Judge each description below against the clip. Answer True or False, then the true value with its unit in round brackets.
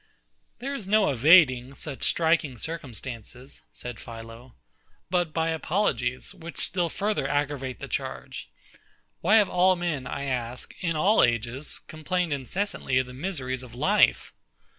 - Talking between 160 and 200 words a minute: False (140 wpm)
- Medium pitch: True (145 Hz)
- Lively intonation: True (5.7 semitones)